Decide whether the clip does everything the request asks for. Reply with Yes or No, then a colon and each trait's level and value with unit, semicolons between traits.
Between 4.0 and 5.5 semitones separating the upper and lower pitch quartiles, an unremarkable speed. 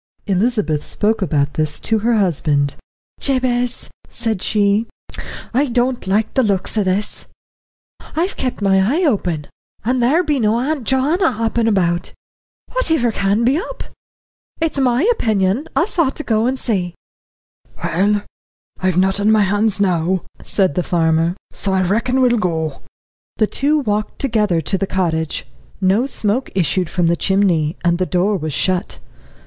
Yes: average, 5.1 semitones; average, 155 wpm